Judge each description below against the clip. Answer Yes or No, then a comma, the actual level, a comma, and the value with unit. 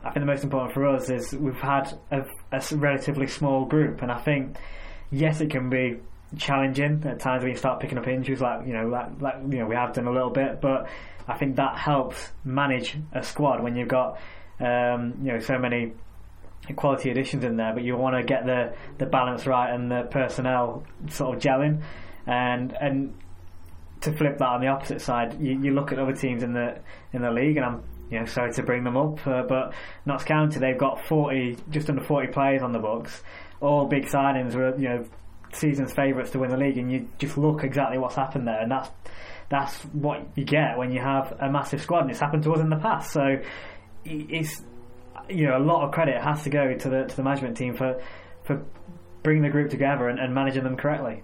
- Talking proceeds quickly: Yes, fast, 220 wpm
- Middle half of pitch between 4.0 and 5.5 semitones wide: No, narrow, 2.4 semitones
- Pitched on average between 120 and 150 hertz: Yes, low, 130 Hz